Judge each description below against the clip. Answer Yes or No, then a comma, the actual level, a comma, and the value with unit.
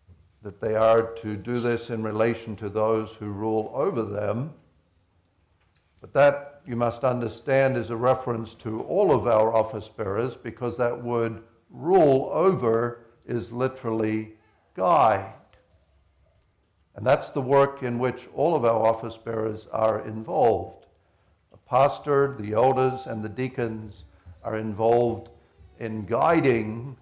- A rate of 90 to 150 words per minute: Yes, slow, 135 wpm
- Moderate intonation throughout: No, narrow, 1.9 semitones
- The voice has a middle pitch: No, low, 115 Hz